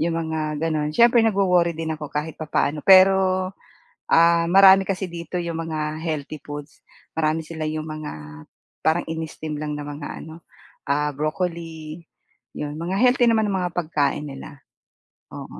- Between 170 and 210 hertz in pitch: No, medium, 160 Hz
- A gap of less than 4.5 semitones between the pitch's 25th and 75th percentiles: Yes, narrow, 2.5 semitones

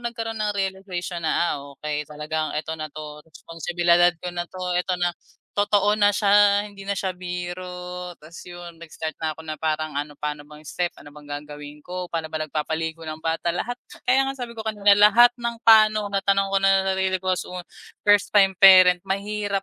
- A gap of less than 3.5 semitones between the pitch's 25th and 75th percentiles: No, average, 4.1 semitones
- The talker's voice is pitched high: No, medium, 180 Hz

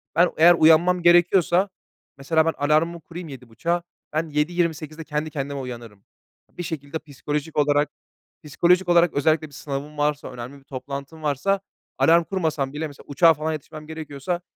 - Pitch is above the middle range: No, medium, 155 Hz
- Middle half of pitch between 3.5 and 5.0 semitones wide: No, average, 2.9 semitones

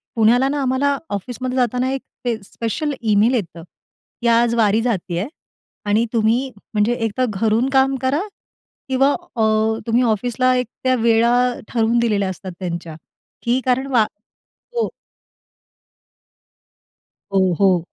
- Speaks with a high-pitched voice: Yes, high, 235 Hz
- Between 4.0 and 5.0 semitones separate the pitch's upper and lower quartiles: No, average, 3.3 semitones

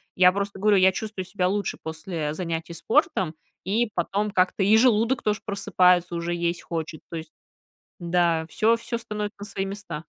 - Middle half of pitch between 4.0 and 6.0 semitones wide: No, average, 3.6 semitones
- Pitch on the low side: No, high, 190 Hz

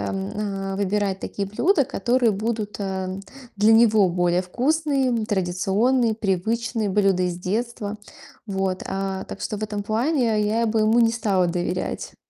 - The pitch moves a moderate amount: Yes, average, 3.1 semitones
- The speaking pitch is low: No, high, 210 Hz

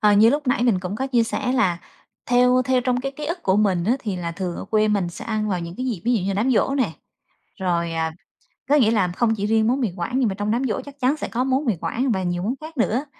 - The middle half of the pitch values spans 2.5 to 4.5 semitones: No, average, 5.1 semitones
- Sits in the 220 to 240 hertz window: Yes, high, 225 Hz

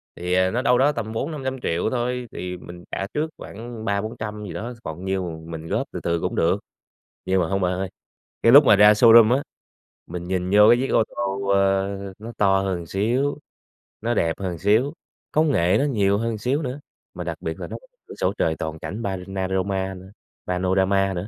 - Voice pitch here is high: No, low, 100 Hz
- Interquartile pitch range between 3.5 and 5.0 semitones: Yes, average, 4.0 semitones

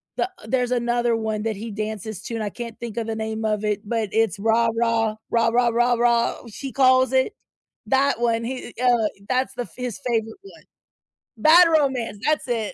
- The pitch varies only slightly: Yes, narrow, 2.2 semitones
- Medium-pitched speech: No, high, 235 Hz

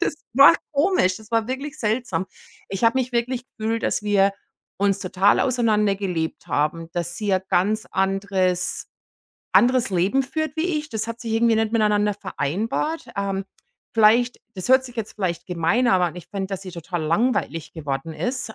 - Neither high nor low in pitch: No, high, 210 Hz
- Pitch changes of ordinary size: Yes, average, 4.6 semitones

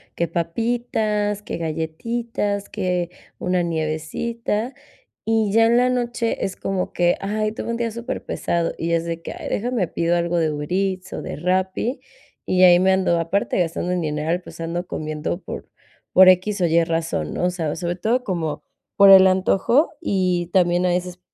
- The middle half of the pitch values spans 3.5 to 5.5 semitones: Yes, average, 3.8 semitones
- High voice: No, medium, 180 Hz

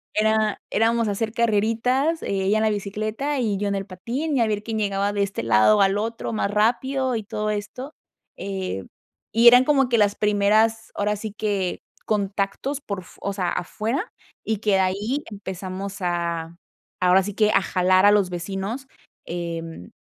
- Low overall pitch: No, high, 210 Hz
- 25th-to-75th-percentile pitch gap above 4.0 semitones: No, average, 2.7 semitones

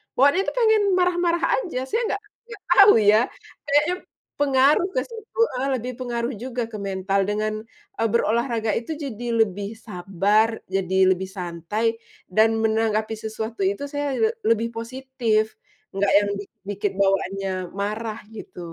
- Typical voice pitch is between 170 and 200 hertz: No, high, 225 Hz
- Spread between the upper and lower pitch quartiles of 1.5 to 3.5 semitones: No, average, 5.2 semitones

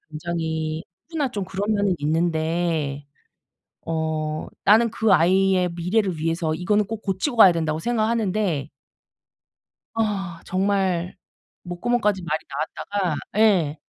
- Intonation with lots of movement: No, average, 4.2 semitones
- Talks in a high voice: No, medium, 180 Hz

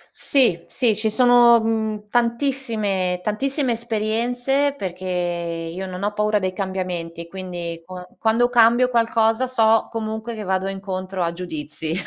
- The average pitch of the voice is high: Yes, high, 210 Hz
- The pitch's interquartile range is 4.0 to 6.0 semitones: Yes, average, 4.3 semitones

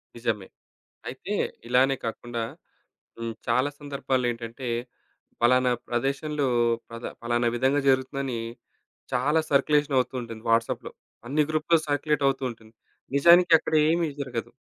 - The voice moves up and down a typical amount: Yes, average, 3.4 semitones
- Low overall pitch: Yes, low, 130 Hz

